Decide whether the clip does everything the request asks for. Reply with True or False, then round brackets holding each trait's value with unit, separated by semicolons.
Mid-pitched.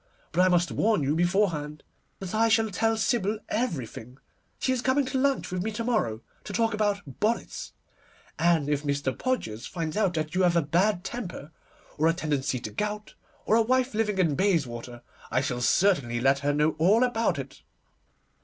True (180 Hz)